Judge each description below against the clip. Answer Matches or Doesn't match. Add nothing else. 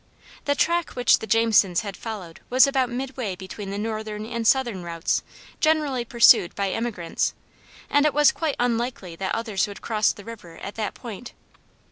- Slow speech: Doesn't match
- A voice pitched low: Doesn't match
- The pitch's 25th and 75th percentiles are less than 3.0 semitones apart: Doesn't match